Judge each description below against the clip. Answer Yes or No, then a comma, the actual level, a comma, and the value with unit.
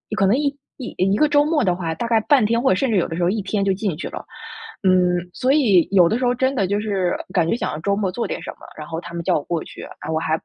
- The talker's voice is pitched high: Yes, high, 200 Hz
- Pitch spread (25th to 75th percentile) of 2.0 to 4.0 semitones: No, average, 5.3 semitones